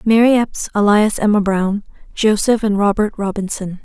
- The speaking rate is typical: No, slow, 125 wpm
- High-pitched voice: Yes, high, 210 Hz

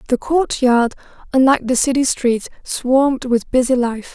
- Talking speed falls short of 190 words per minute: Yes, average, 160 wpm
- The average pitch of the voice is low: No, very high, 255 Hz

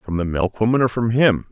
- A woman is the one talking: No, male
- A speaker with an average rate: No, fast, 240 wpm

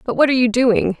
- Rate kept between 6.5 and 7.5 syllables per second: Yes, 6.7 syllables/s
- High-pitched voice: Yes, high, 240 Hz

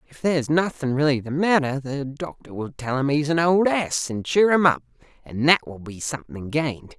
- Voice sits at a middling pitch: Yes, medium, 145 Hz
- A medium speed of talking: No, fast, 215 wpm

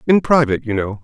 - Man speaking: Yes, male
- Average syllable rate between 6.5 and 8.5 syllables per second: Yes, 6.7 syllables/s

